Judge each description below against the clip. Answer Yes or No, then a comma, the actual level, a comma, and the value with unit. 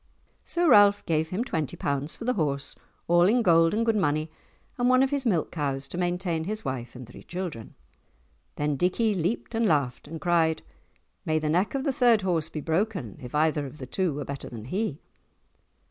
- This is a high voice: No, medium, 165 Hz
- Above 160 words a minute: Yes, average, 200 wpm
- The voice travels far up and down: Yes, wide, 6.0 semitones